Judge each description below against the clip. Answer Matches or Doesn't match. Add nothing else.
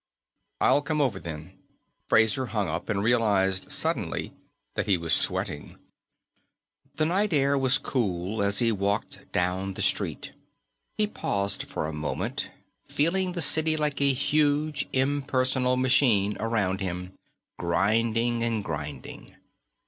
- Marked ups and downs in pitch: Matches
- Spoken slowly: Matches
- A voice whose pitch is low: Matches